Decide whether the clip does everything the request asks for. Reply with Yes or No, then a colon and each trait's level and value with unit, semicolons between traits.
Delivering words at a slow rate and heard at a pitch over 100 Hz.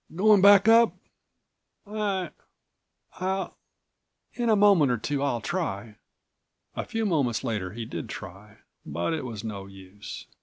Yes: slow, 125 wpm; medium, 140 Hz